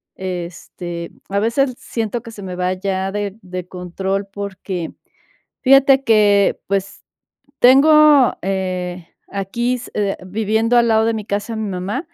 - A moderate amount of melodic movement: Yes, average, 3.6 semitones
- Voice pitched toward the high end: Yes, high, 200 Hz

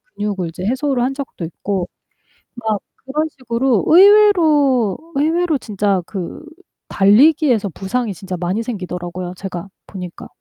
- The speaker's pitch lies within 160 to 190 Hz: No, high, 220 Hz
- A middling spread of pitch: No, wide, 6.8 semitones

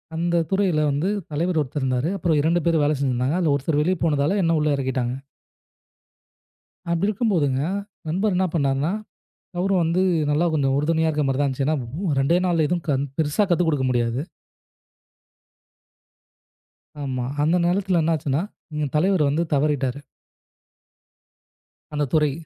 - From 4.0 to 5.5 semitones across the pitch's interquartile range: No, average, 3.6 semitones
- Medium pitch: Yes, medium, 155 Hz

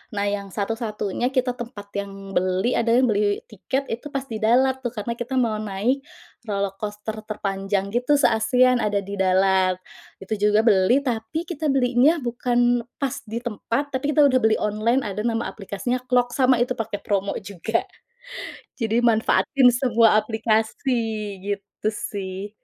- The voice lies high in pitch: Yes, high, 225 Hz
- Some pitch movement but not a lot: Yes, average, 3.6 semitones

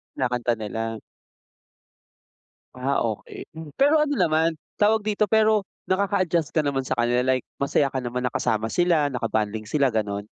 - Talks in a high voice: No, low, 135 Hz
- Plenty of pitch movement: Yes, wide, 7.1 semitones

